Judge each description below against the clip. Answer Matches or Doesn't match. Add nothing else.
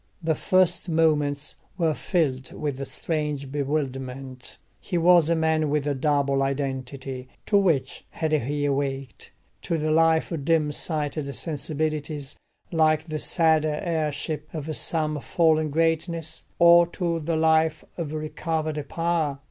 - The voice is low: Doesn't match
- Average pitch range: Doesn't match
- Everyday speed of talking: Doesn't match